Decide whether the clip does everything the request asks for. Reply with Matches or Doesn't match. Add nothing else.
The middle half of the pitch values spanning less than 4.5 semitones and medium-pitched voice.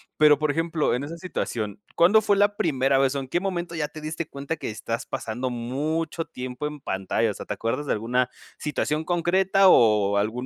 Doesn't match